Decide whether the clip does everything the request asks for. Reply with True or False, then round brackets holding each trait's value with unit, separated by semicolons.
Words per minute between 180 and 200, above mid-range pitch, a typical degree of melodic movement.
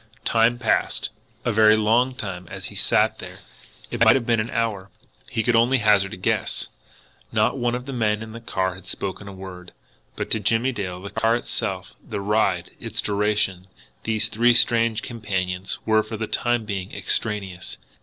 False (185 wpm; 110 Hz; 3.0 semitones)